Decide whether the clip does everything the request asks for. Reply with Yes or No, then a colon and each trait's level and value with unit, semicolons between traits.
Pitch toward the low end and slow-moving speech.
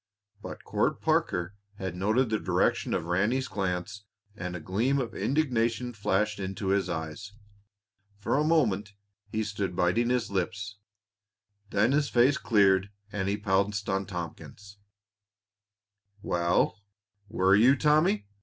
Yes: low, 100 Hz; slow, 130 wpm